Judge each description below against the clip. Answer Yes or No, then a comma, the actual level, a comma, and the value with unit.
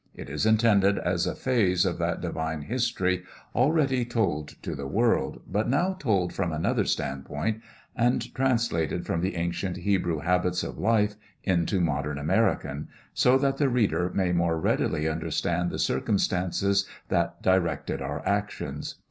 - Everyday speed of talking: Yes, average, 150 wpm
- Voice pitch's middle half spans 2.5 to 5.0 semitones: No, wide, 5.4 semitones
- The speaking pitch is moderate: No, very low, 95 Hz